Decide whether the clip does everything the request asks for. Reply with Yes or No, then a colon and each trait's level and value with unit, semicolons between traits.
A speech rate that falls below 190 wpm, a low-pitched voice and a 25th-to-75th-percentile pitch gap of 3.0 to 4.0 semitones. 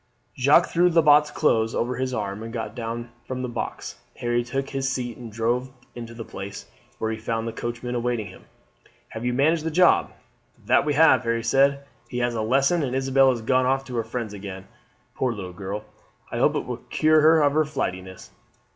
No: fast, 205 wpm; low, 125 Hz; average, 3.3 semitones